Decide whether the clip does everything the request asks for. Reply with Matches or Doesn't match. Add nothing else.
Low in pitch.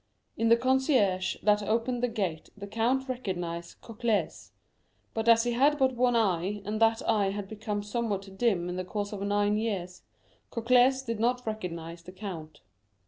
Doesn't match